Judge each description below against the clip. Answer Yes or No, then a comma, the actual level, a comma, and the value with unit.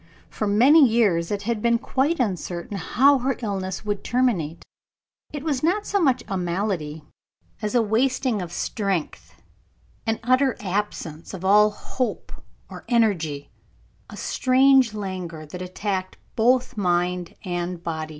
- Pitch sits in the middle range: No, high, 205 Hz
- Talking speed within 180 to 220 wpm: No, average, 140 wpm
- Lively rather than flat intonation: Yes, wide, 5.8 semitones